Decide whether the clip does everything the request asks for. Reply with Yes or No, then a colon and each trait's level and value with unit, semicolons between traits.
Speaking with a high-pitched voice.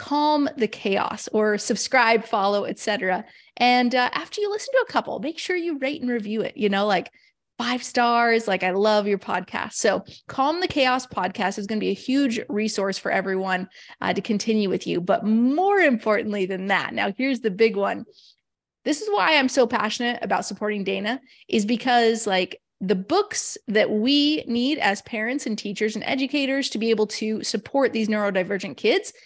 Yes: high, 225 Hz